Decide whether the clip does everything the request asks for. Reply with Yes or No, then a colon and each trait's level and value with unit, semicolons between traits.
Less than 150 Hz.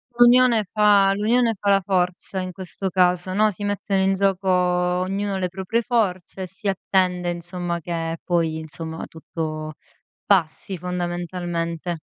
No: medium, 185 Hz